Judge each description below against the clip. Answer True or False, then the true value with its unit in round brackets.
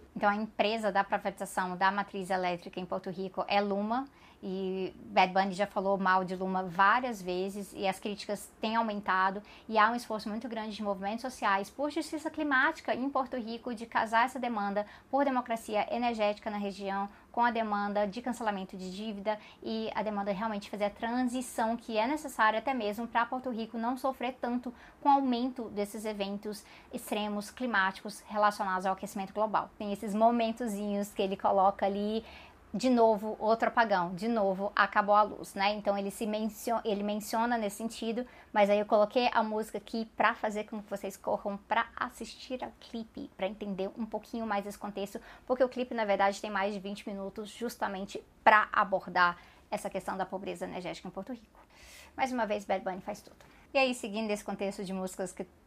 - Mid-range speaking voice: False (210 Hz)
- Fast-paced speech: True (190 wpm)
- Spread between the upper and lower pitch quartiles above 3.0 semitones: False (2.6 semitones)